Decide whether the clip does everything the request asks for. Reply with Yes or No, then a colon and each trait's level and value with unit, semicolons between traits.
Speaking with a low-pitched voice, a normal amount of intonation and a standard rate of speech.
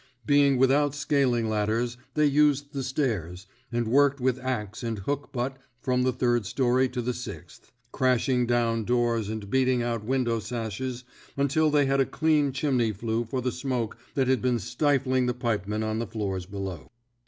Yes: low, 125 Hz; average, 3.0 semitones; average, 175 wpm